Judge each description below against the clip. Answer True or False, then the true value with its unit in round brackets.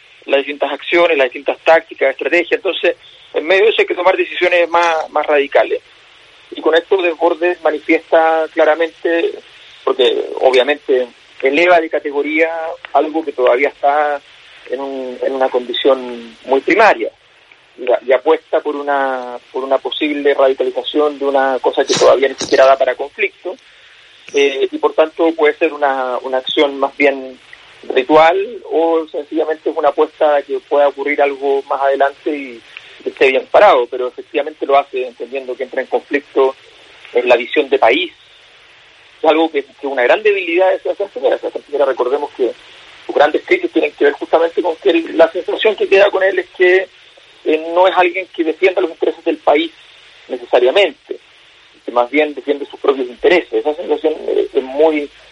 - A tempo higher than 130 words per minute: True (170 wpm)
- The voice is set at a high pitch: False (160 Hz)